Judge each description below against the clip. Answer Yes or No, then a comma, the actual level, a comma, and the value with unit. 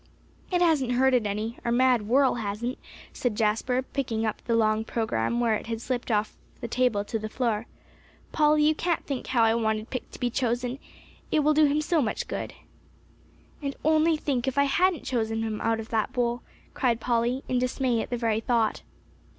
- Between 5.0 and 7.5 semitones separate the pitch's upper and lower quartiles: No, average, 3.1 semitones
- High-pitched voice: Yes, high, 240 Hz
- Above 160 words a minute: Yes, average, 200 wpm